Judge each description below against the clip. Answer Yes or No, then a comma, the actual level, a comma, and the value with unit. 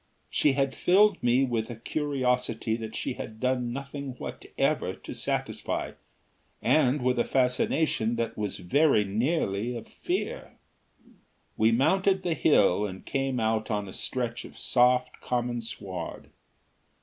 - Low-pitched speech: Yes, low, 125 Hz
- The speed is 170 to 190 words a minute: No, slow, 135 wpm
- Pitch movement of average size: Yes, average, 3.6 semitones